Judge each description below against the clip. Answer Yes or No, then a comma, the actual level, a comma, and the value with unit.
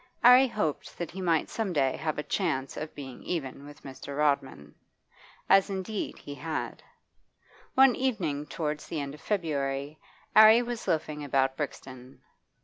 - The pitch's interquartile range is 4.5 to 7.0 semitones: Yes, wide, 5.5 semitones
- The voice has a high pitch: No, medium, 150 Hz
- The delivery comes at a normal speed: Yes, average, 150 wpm